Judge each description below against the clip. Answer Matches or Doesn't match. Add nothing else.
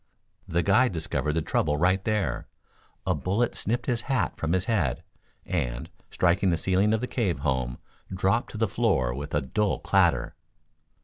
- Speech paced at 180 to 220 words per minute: Doesn't match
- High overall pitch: Doesn't match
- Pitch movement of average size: Doesn't match